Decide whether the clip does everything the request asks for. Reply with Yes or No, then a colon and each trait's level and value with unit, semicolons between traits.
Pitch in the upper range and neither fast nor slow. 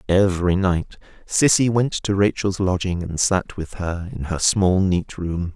No: very low, 95 Hz; average, 175 wpm